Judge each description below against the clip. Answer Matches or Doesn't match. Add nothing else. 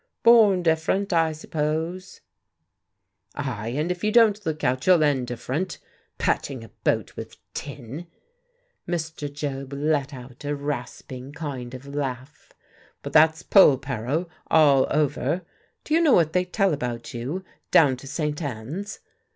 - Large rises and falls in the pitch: Doesn't match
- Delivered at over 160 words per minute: Doesn't match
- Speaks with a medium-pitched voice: Matches